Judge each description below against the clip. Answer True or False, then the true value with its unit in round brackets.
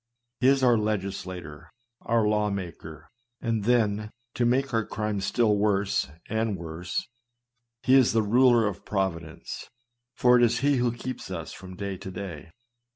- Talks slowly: False (160 wpm)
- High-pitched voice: False (105 Hz)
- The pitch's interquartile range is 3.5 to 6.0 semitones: True (3.8 semitones)